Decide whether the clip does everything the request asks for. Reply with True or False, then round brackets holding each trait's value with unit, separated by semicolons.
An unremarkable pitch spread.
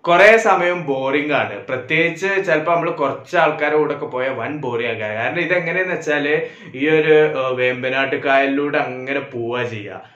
True (4.4 semitones)